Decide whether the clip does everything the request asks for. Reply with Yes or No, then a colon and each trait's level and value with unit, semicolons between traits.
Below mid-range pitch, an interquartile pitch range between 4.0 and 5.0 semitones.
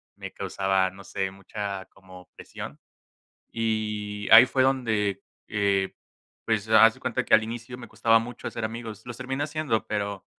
No: low, 110 Hz; average, 2.9 semitones